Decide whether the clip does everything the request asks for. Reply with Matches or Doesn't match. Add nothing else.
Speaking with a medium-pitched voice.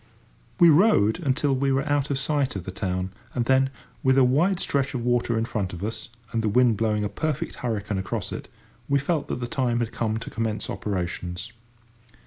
Doesn't match